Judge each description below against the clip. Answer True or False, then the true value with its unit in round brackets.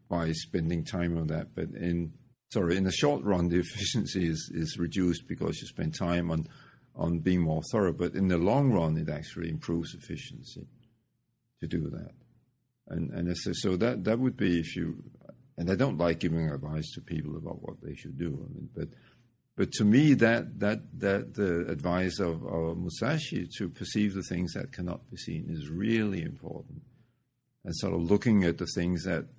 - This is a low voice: True (90 Hz)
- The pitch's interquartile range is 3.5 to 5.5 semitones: True (4.8 semitones)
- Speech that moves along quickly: False (195 wpm)